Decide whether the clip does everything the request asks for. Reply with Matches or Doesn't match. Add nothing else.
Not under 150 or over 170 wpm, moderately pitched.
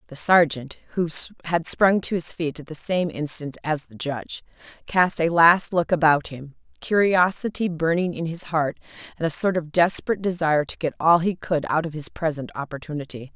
Doesn't match